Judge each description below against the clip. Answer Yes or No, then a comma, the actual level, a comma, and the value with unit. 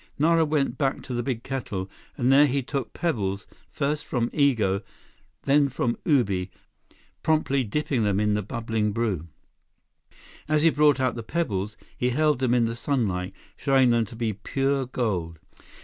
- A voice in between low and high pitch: No, low, 125 Hz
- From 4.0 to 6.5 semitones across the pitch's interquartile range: Yes, average, 4.9 semitones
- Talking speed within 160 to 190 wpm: Yes, average, 165 wpm